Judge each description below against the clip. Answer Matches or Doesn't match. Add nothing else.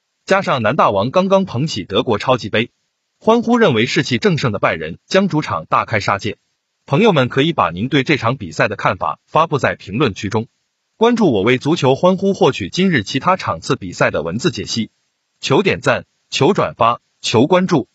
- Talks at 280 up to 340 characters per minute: Matches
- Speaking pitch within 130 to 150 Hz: Matches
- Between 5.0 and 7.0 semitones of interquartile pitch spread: Doesn't match